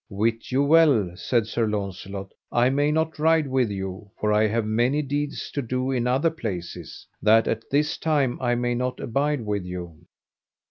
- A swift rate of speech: No, average, 180 wpm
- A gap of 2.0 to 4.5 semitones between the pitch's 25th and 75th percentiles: No, average, 5.1 semitones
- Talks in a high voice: No, low, 120 Hz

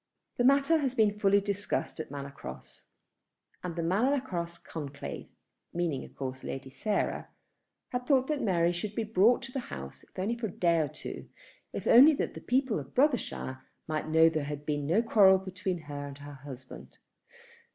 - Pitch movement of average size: No, wide, 8.1 semitones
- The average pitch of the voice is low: No, medium, 180 Hz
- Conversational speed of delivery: Yes, average, 185 wpm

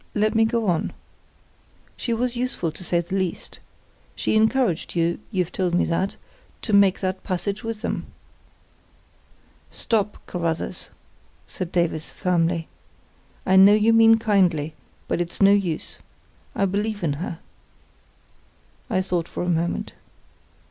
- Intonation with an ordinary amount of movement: Yes, average, 3.9 semitones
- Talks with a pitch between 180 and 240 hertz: Yes, high, 190 Hz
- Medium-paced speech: No, slow, 130 wpm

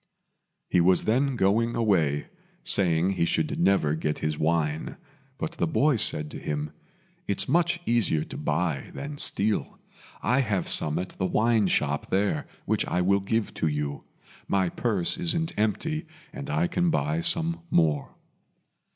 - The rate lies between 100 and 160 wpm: Yes, average, 155 wpm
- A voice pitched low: Yes, low, 100 Hz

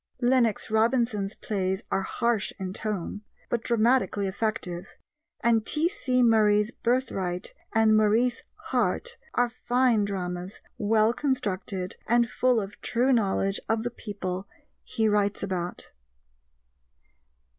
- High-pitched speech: Yes, high, 220 Hz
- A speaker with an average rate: No, slow, 115 wpm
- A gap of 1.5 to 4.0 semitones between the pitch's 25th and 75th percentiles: Yes, average, 3.4 semitones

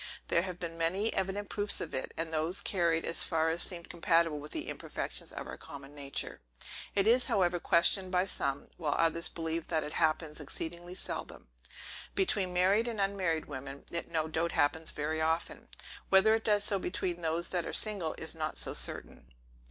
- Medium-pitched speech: Yes, medium, 170 Hz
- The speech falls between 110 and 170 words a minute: No, average, 185 wpm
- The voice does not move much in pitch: No, average, 3.0 semitones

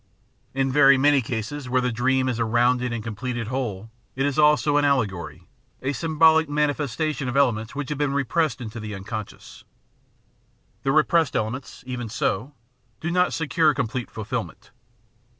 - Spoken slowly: No, average, 160 wpm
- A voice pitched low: Yes, low, 130 Hz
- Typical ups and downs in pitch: Yes, average, 4.2 semitones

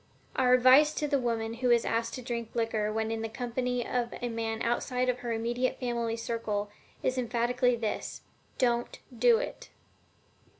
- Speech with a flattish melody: Yes, narrow, 1.7 semitones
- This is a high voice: Yes, high, 240 Hz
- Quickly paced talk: No, average, 170 wpm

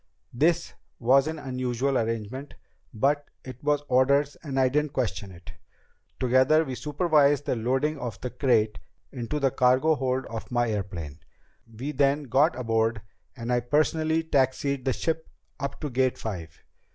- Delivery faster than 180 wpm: No, average, 150 wpm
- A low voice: Yes, low, 130 Hz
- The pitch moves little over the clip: No, average, 3.5 semitones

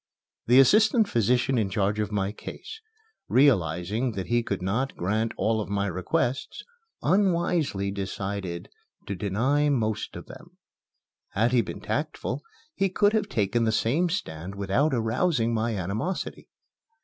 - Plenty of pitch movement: Yes, wide, 5.7 semitones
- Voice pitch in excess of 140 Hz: No, low, 115 Hz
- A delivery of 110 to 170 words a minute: Yes, average, 140 wpm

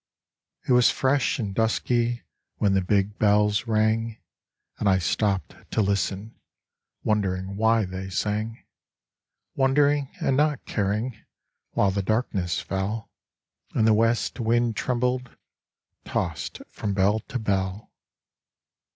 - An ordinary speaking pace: No, slow, 115 wpm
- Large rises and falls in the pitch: No, average, 3.2 semitones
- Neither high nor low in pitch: No, low, 110 Hz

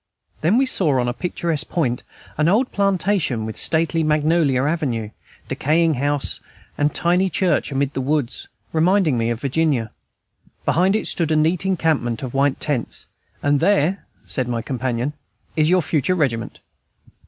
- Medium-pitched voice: Yes, medium, 150 Hz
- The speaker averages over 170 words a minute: No, average, 155 wpm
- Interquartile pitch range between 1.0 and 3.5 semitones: No, average, 4.7 semitones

